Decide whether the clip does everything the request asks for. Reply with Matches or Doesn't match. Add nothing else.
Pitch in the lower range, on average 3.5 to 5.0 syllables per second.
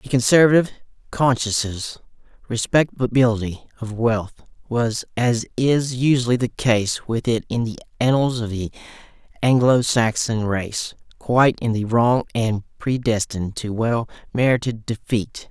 Matches